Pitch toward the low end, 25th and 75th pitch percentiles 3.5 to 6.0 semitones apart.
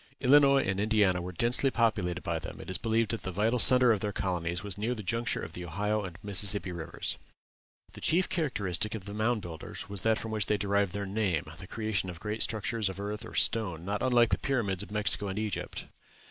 No: low, 105 Hz; average, 3.1 semitones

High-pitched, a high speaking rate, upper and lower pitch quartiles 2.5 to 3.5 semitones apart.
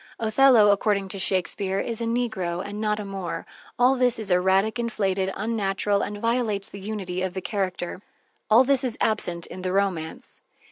No: high, 200 Hz; average, 175 wpm; average, 3.0 semitones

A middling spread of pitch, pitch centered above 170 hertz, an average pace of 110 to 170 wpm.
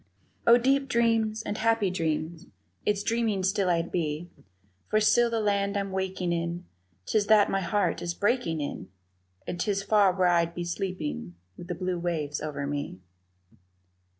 Yes: average, 3.9 semitones; high, 190 Hz; average, 160 wpm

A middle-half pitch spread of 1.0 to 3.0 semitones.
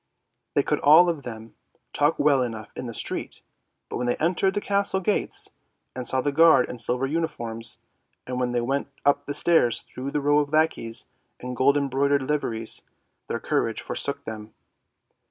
No: average, 3.6 semitones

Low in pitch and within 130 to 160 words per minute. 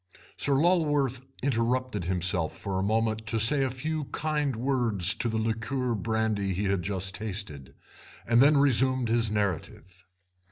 Yes: low, 115 Hz; average, 150 wpm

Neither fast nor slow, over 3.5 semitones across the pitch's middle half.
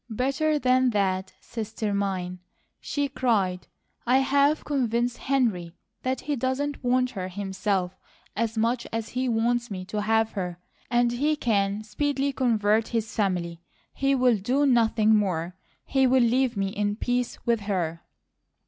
Yes: average, 150 wpm; average, 4.3 semitones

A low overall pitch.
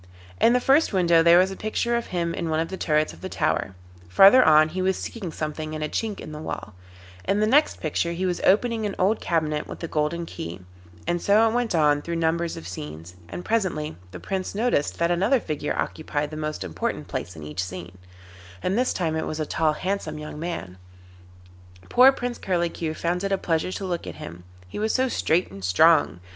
No: medium, 170 Hz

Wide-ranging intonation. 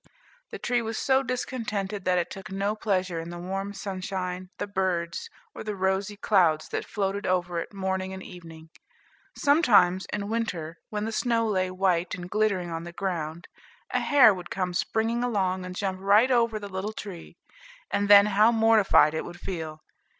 No: average, 2.9 semitones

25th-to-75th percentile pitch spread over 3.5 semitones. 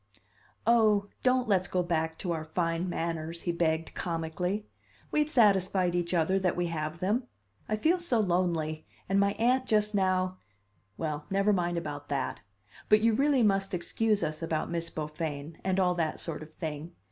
Yes: average, 4.1 semitones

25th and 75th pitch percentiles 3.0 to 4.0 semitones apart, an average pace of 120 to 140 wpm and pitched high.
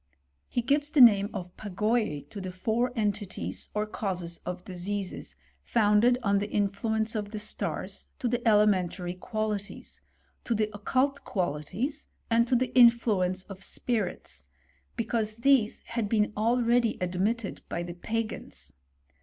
Yes: average, 3.3 semitones; slow, 135 wpm; high, 215 Hz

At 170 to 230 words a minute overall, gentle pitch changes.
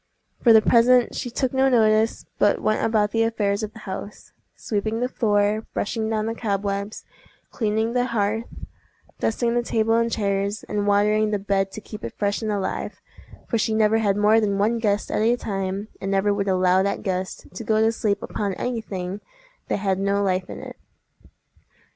Yes: average, 190 wpm; narrow, 2.0 semitones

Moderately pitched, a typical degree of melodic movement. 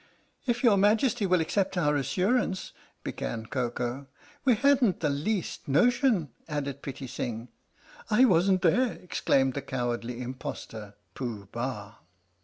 No: medium, 150 Hz; wide, 9.0 semitones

